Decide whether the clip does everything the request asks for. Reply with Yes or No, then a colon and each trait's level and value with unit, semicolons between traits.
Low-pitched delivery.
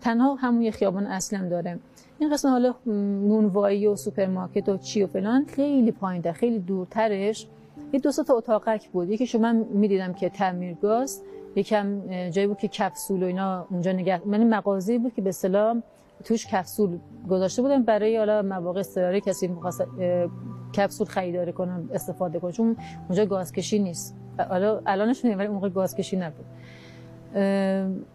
No: high, 200 Hz